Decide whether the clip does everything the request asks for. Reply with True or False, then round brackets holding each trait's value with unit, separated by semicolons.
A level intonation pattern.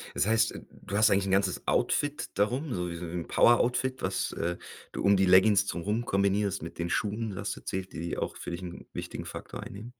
False (3.2 semitones)